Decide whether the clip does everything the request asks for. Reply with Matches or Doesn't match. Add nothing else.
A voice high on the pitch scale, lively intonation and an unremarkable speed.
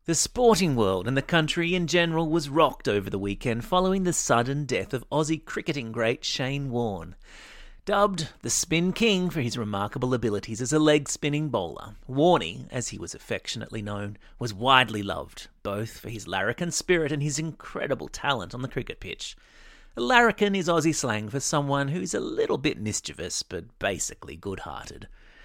Doesn't match